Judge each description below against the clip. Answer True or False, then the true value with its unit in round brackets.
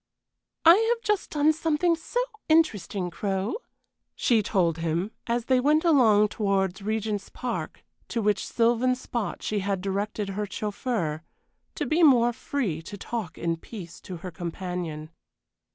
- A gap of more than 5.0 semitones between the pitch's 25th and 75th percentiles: True (5.4 semitones)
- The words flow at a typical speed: True (145 wpm)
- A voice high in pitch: True (210 Hz)